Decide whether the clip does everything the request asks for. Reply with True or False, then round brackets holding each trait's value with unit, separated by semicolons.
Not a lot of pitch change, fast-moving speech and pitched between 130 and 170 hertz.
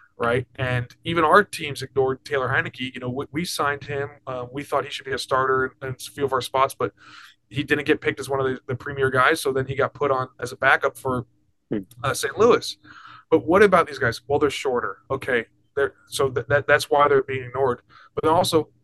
True (1.7 semitones; 240 wpm; 135 Hz)